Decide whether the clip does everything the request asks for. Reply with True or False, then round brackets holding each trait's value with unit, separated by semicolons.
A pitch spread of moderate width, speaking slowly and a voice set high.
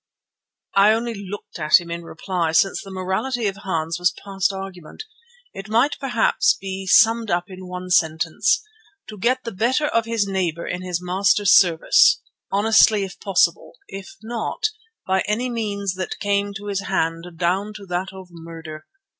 False (3.0 semitones; 165 wpm; 195 Hz)